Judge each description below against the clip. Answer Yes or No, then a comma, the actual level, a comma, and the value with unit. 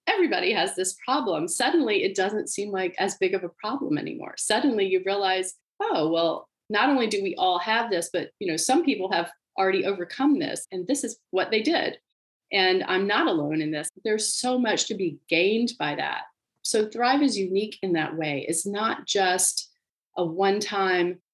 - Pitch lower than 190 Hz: No, high, 200 Hz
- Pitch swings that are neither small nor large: No, wide, 5.8 semitones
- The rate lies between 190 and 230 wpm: Yes, average, 195 wpm